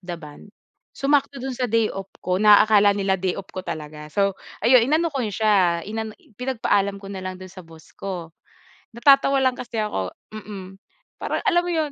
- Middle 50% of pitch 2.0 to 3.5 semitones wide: No, average, 5.2 semitones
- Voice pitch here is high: Yes, high, 200 Hz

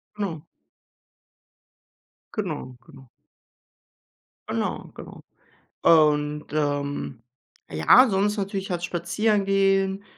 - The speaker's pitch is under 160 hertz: No, medium, 180 Hz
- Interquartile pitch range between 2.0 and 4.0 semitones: No, average, 5.0 semitones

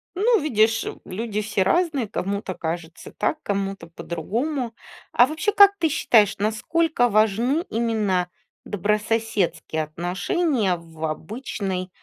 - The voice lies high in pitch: Yes, high, 215 Hz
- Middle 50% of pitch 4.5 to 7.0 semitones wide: Yes, wide, 5.6 semitones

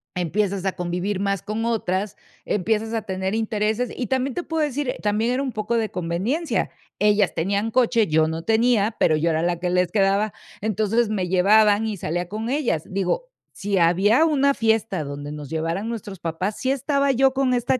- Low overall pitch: No, high, 210 Hz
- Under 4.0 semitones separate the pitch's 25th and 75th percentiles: No, average, 4.4 semitones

